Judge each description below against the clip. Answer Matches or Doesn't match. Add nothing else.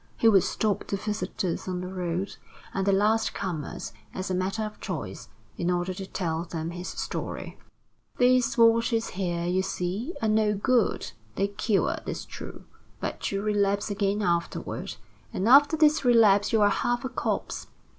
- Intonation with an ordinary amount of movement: Matches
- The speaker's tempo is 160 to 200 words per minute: Matches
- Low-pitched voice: Doesn't match